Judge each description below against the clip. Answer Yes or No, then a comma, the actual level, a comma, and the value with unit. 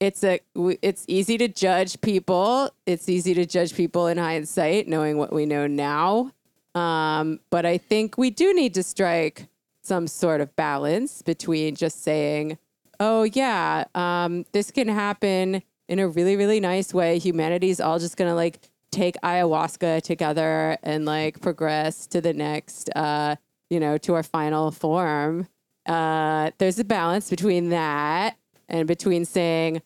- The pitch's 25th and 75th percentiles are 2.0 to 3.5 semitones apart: Yes, average, 3.2 semitones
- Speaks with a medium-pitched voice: Yes, medium, 175 Hz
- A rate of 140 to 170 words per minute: Yes, average, 155 wpm